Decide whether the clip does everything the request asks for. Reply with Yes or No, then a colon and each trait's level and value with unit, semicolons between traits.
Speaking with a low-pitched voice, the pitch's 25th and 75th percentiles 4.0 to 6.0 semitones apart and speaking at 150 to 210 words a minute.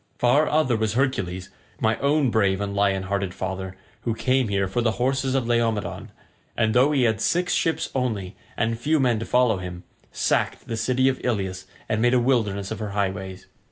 Yes: low, 115 Hz; average, 4.4 semitones; average, 195 wpm